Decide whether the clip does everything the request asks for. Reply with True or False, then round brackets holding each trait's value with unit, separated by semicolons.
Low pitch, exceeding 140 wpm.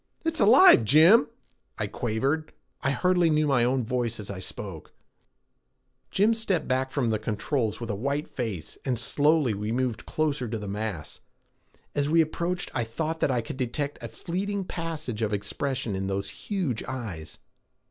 True (130 Hz; 170 wpm)